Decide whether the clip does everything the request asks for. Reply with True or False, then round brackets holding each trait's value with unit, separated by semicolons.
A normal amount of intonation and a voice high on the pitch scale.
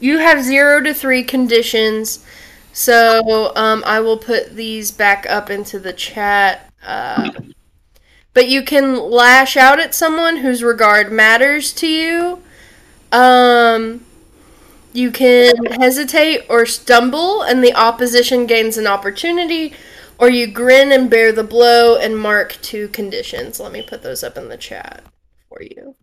True (4.3 semitones; 245 Hz)